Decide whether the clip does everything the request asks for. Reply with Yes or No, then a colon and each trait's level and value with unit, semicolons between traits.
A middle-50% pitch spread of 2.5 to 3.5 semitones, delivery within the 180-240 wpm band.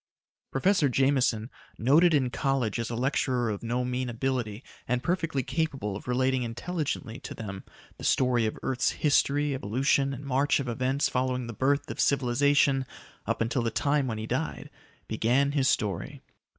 No: average, 3.0 semitones; average, 165 wpm